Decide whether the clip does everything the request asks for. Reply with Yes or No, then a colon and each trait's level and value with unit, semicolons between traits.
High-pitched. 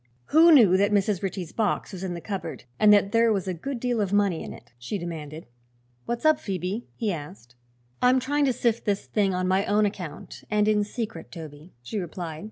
Yes: high, 200 Hz